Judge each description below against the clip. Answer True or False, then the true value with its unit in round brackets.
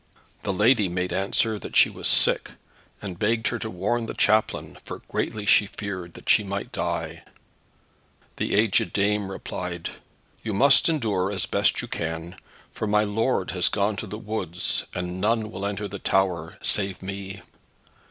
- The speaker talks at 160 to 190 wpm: True (170 wpm)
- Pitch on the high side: False (100 Hz)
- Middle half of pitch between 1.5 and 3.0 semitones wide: True (2.7 semitones)